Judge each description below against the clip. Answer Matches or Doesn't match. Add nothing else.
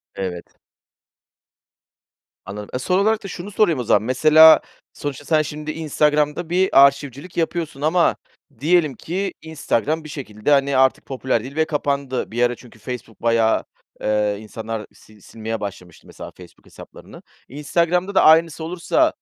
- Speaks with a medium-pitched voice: Matches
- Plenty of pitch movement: Matches